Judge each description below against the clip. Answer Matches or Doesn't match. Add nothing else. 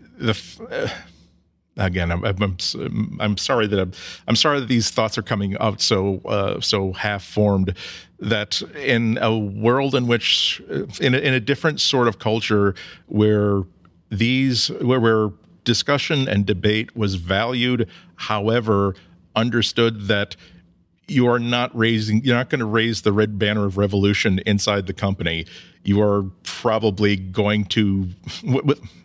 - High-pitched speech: Doesn't match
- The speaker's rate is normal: Matches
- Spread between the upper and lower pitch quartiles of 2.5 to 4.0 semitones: Matches